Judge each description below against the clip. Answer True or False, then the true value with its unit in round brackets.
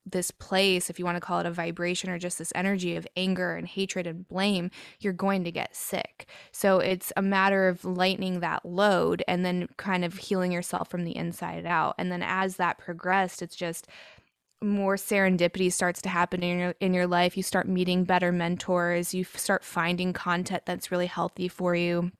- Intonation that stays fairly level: True (1.3 semitones)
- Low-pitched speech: False (180 Hz)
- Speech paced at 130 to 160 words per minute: False (200 wpm)